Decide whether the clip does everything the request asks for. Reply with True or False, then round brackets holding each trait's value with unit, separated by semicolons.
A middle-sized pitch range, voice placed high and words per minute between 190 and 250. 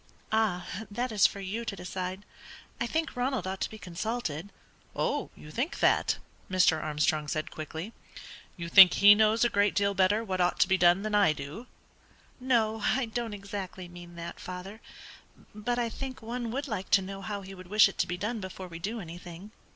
True (3.7 semitones; 200 Hz; 195 wpm)